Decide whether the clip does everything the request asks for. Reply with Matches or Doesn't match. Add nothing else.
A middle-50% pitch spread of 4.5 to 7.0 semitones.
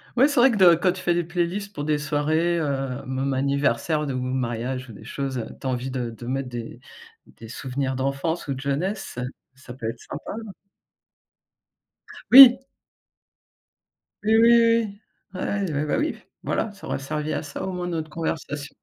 Matches